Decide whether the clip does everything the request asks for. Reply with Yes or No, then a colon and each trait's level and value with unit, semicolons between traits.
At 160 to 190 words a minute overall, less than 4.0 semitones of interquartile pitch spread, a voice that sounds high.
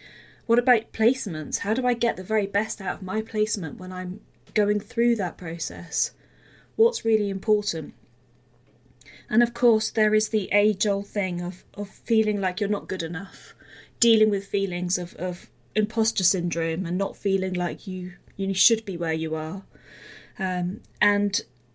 Yes: average, 165 wpm; average, 3.3 semitones; high, 200 Hz